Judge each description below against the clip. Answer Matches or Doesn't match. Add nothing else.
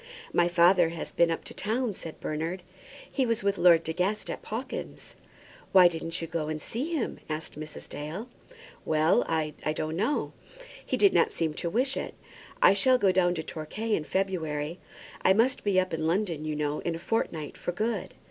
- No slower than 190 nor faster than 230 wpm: Matches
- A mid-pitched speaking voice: Matches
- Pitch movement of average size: Matches